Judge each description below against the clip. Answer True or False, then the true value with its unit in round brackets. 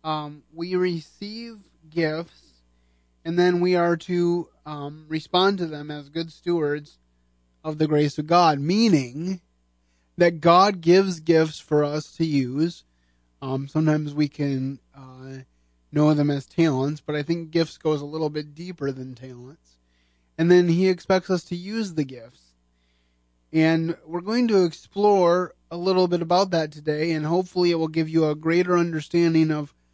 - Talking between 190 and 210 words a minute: False (160 wpm)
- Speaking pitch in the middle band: True (155 Hz)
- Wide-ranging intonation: False (4.2 semitones)